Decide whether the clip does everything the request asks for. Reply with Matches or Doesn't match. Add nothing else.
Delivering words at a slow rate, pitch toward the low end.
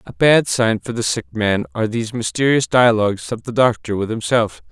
Doesn't match